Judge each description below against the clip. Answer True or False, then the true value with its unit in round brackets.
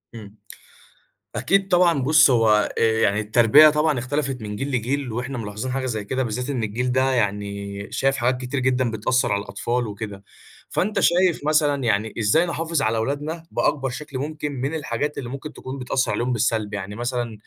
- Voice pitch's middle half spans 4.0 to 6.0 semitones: True (4.5 semitones)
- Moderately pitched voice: False (125 Hz)